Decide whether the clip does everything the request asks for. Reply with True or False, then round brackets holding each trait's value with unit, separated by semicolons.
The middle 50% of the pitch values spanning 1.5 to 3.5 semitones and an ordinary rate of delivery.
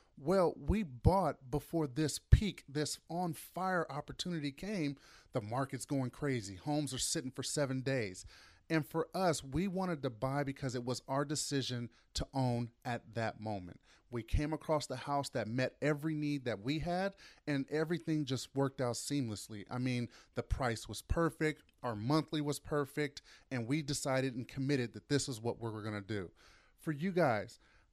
False (4.0 semitones; 180 wpm)